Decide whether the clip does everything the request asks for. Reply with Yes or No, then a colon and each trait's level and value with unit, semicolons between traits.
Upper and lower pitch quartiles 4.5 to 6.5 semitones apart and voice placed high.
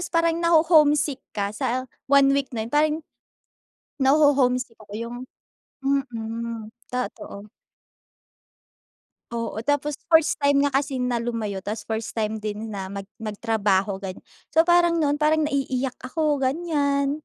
Yes: average, 4.9 semitones; very high, 260 Hz